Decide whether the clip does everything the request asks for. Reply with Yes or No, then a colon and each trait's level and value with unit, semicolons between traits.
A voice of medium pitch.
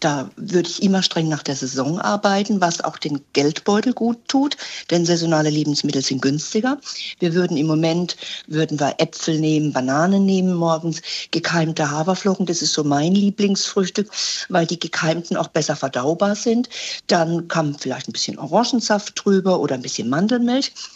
Yes: medium, 170 Hz